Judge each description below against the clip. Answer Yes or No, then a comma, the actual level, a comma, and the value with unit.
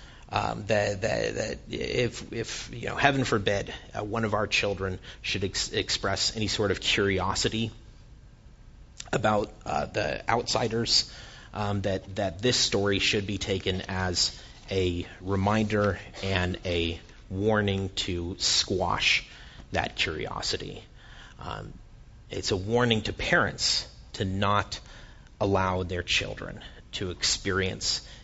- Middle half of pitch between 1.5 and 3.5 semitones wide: Yes, narrow, 2.4 semitones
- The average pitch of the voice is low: Yes, low, 100 Hz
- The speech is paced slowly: Yes, slow, 120 wpm